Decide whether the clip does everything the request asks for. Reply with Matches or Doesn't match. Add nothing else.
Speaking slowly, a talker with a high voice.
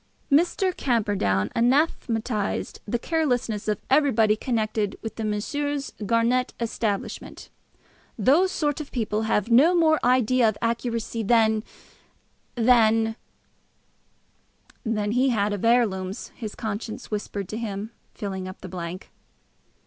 Matches